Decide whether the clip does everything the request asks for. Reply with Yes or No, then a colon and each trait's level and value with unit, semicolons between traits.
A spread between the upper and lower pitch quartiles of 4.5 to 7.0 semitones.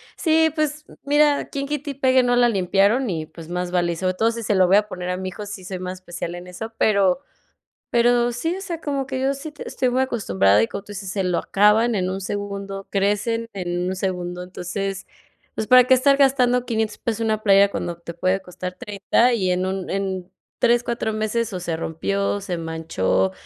Yes: average, 4.9 semitones